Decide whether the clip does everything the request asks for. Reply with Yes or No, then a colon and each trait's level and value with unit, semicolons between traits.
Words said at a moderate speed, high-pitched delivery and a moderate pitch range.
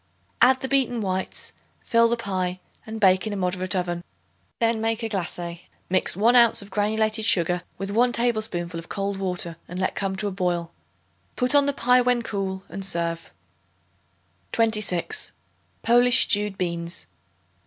Yes: average, 160 wpm; high, 200 Hz; average, 4.2 semitones